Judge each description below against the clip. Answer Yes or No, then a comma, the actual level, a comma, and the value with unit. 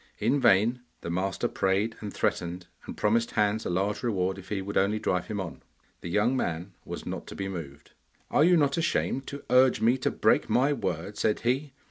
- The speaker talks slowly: No, fast, 205 wpm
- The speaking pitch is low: Yes, low, 105 Hz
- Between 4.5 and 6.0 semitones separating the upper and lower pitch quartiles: Yes, average, 4.8 semitones